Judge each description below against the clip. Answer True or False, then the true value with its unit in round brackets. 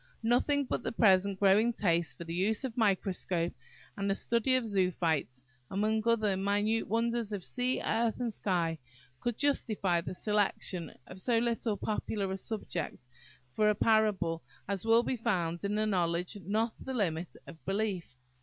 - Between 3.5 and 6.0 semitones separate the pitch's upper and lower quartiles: True (3.8 semitones)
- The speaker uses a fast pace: False (165 wpm)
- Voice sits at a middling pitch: False (205 Hz)